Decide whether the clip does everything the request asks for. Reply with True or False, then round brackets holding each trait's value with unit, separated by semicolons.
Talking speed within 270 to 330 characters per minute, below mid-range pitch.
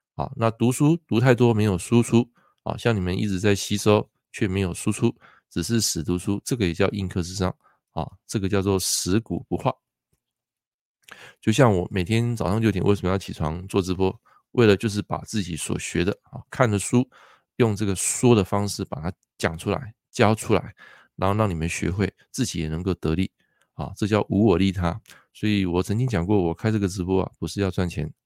True (285 characters per minute; 100 Hz)